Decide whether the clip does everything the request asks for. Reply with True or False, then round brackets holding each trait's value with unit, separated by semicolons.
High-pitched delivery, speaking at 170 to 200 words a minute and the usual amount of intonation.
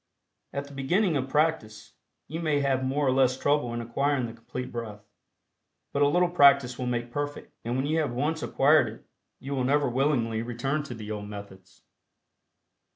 False (135 Hz; 185 wpm; 3.6 semitones)